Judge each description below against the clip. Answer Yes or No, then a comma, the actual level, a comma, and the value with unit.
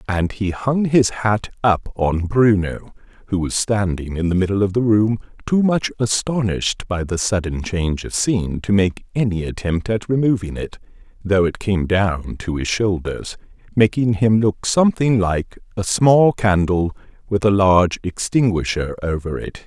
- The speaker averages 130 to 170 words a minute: Yes, average, 165 wpm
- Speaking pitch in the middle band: No, low, 100 Hz